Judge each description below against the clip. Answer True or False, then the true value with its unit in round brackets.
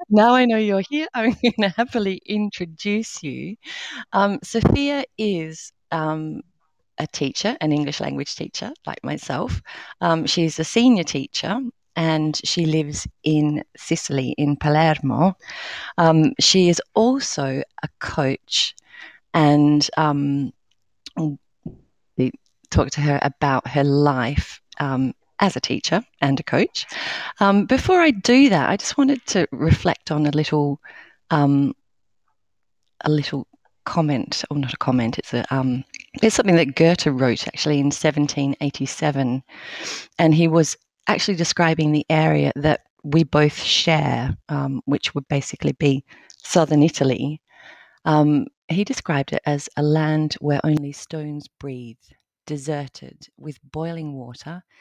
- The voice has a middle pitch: True (155 Hz)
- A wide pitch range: False (4.0 semitones)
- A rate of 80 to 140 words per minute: True (135 wpm)